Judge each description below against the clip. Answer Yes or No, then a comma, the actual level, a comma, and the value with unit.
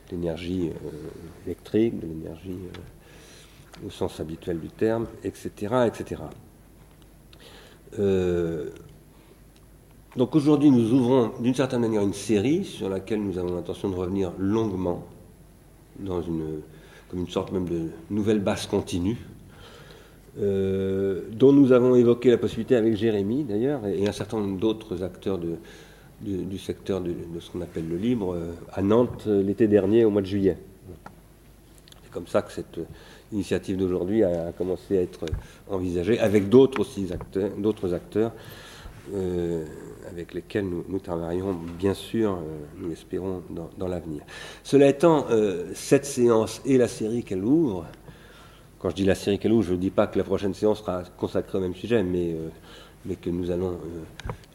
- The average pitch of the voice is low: Yes, very low, 95 Hz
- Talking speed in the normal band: Yes, average, 165 wpm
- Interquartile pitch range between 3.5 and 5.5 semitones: Yes, average, 3.9 semitones